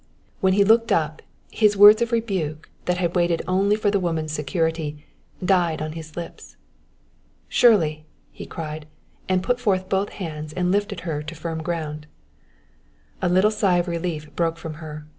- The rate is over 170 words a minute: No, average, 165 wpm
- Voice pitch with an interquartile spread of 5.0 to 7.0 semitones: No, average, 3.9 semitones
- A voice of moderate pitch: Yes, medium, 170 Hz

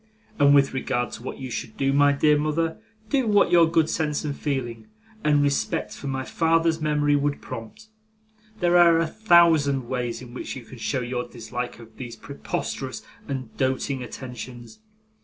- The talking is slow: No, average, 175 wpm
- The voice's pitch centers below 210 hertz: Yes, medium, 140 Hz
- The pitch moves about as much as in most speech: Yes, average, 4.4 semitones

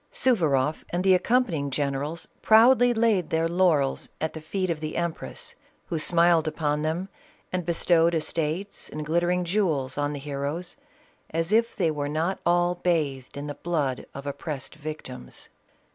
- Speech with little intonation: No, average, 3.3 semitones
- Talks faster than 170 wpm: No, average, 165 wpm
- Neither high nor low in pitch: Yes, medium, 165 Hz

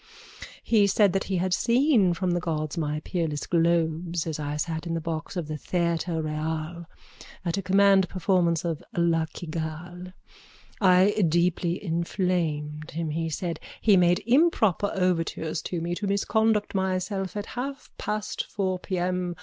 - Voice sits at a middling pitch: Yes, medium, 175 Hz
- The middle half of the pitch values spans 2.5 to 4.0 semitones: Yes, average, 2.9 semitones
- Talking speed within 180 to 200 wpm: No, average, 150 wpm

